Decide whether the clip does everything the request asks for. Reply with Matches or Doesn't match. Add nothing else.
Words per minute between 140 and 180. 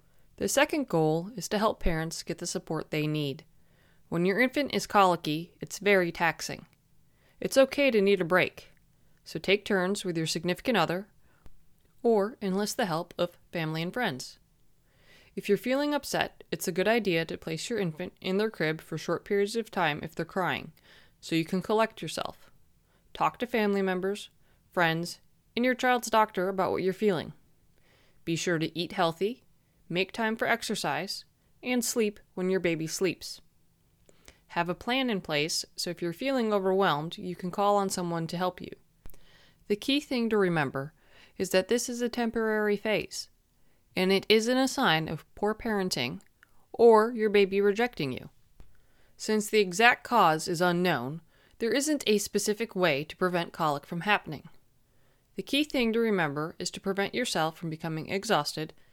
Matches